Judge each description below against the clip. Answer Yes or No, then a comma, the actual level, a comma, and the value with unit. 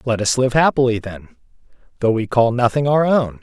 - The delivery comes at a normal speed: Yes, average, 195 wpm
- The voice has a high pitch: No, low, 120 Hz